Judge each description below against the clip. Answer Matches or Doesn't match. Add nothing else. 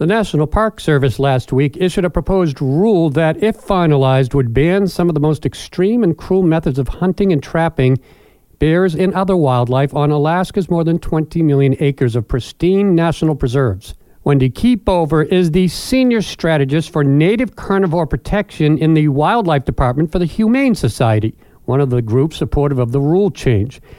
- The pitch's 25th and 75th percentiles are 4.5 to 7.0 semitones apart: Matches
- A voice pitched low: Doesn't match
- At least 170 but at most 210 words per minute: Matches